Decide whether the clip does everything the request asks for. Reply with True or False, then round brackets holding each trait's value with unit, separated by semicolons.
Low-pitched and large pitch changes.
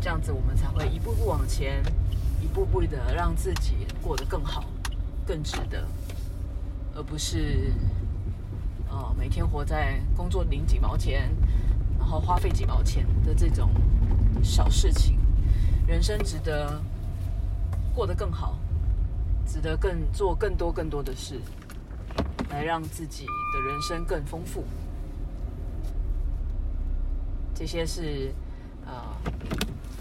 False (90 Hz; 2.4 semitones)